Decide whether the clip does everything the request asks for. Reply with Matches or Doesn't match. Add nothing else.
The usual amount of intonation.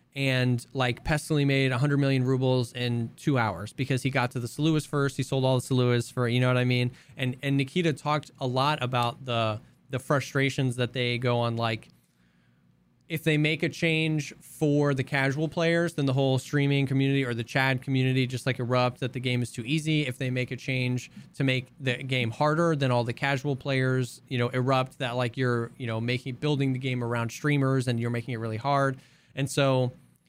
Doesn't match